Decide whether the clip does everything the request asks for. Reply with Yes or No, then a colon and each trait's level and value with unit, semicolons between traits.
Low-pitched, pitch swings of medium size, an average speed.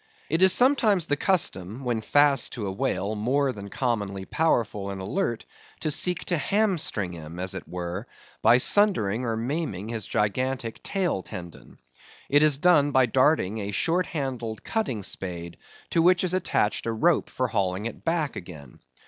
No: low, 120 Hz; wide, 8.3 semitones; average, 165 wpm